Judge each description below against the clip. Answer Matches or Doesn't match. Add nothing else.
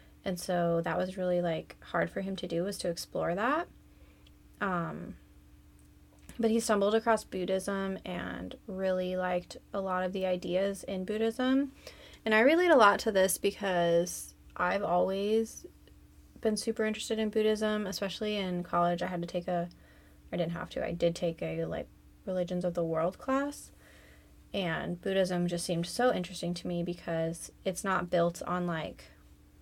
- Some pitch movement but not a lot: Matches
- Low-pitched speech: Doesn't match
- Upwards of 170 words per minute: Doesn't match